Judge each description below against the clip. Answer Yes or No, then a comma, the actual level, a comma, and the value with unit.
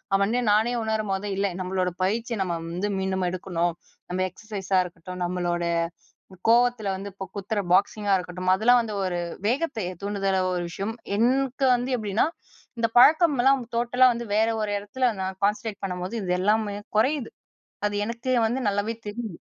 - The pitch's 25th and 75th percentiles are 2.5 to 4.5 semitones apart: Yes, average, 3.8 semitones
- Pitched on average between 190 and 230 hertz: Yes, high, 205 Hz